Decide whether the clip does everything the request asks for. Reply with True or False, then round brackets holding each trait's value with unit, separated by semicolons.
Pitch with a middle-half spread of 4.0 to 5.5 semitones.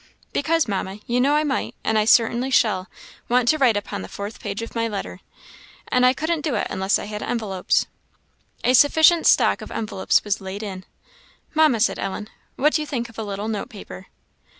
True (4.8 semitones)